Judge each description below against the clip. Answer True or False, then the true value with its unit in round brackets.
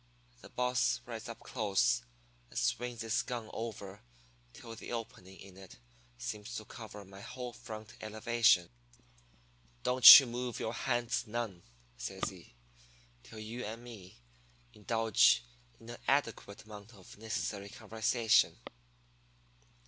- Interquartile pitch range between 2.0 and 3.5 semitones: True (2.5 semitones)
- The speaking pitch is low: True (115 Hz)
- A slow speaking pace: True (125 wpm)